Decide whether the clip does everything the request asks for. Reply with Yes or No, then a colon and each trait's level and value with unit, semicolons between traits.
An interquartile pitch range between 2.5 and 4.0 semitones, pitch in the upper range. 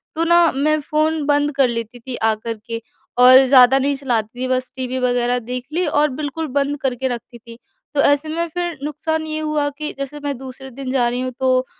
Yes: average, 3.3 semitones; very high, 270 Hz